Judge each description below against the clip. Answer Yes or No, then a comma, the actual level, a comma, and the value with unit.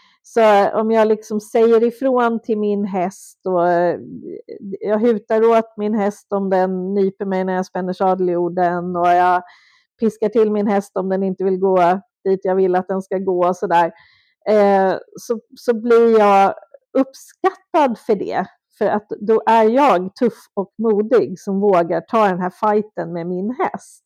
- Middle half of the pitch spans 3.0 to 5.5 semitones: Yes, average, 3.3 semitones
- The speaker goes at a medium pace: Yes, average, 170 wpm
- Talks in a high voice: Yes, high, 205 Hz